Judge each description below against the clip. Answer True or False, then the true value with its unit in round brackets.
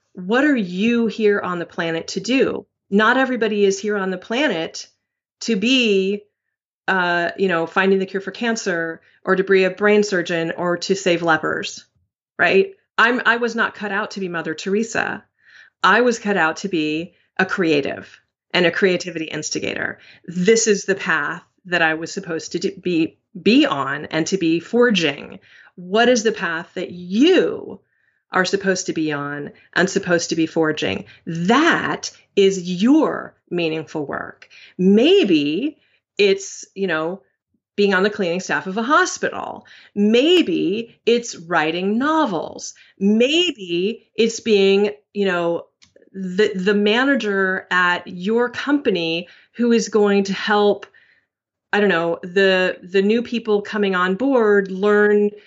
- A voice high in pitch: True (195 Hz)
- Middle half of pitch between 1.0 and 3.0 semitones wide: False (4.3 semitones)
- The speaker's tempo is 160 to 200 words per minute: False (150 wpm)